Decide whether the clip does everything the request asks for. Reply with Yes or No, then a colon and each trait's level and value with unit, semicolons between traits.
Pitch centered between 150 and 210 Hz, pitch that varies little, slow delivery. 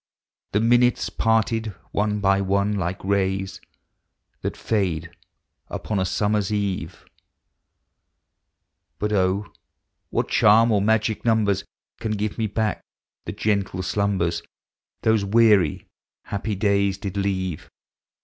No: low, 100 Hz; narrow, 2.0 semitones; slow, 115 wpm